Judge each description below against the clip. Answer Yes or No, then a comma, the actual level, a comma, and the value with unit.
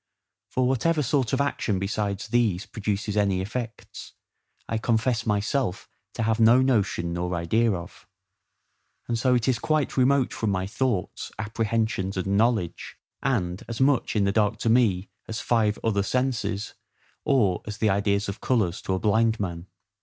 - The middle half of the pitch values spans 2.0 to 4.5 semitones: Yes, average, 3.5 semitones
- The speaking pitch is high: No, low, 110 Hz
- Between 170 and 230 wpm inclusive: No, average, 160 wpm